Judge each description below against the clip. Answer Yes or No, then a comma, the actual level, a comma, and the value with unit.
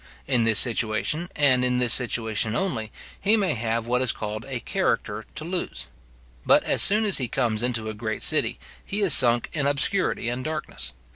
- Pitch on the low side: Yes, low, 125 Hz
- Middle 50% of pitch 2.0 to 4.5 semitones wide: No, average, 5.2 semitones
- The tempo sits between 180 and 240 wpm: Yes, average, 190 wpm